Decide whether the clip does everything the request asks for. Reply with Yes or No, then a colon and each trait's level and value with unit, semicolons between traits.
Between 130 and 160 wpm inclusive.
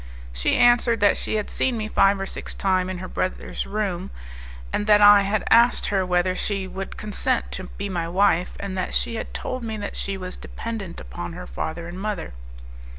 No: average, 200 wpm